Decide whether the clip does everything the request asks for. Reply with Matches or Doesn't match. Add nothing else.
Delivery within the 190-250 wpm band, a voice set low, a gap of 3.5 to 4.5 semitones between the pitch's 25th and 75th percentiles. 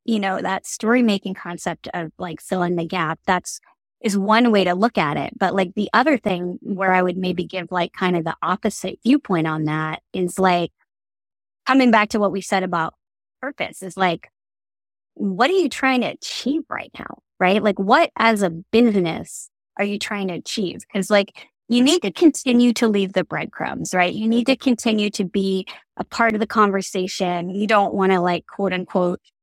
Doesn't match